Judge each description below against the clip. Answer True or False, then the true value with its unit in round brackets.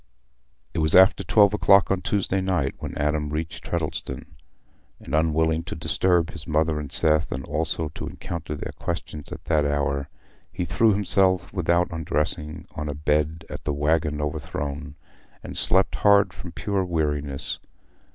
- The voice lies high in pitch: False (80 Hz)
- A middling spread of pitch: True (3.0 semitones)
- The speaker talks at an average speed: True (155 wpm)